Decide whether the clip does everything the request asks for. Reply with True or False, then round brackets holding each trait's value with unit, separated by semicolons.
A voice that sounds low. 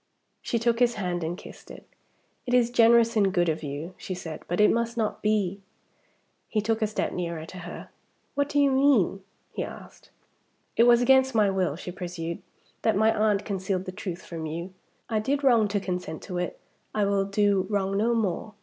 False (200 Hz)